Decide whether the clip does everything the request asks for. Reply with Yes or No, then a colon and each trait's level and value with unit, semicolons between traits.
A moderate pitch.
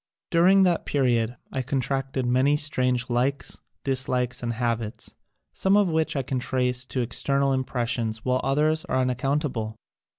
No: low, 130 Hz